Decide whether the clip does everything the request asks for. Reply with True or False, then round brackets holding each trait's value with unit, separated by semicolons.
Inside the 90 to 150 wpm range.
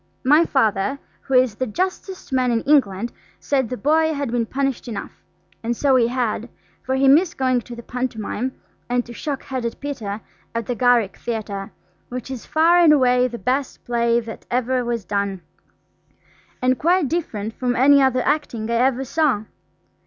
False (170 wpm)